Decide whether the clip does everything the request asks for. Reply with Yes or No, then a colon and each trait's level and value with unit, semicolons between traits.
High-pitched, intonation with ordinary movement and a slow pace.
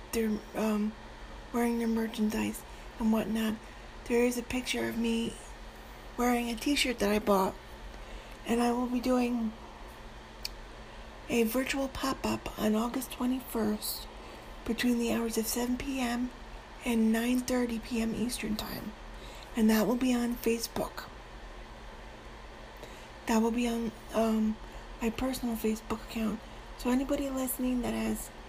No: high, 230 Hz; narrow, 2.0 semitones; slow, 130 wpm